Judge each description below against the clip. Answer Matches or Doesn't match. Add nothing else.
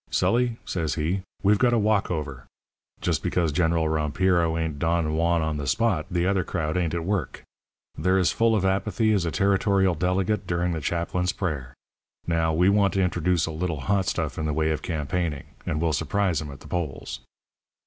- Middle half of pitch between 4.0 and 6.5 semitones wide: Doesn't match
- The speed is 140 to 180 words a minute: Doesn't match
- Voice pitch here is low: Matches